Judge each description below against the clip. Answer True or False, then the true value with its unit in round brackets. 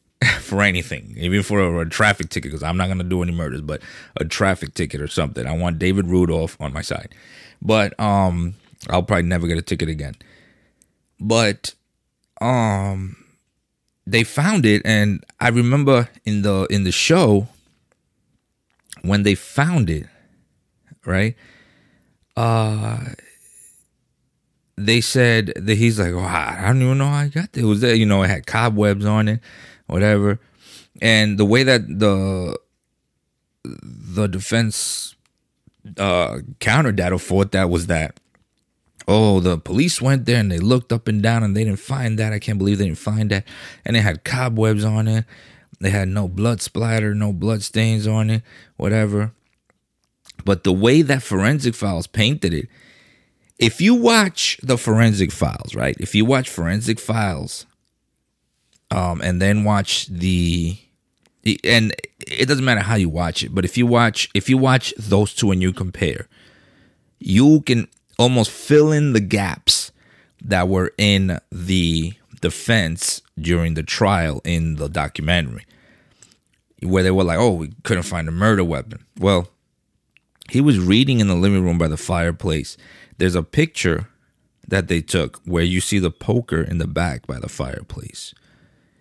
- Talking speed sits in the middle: True (160 wpm)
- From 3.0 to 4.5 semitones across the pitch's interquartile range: True (4.2 semitones)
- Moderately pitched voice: False (100 Hz)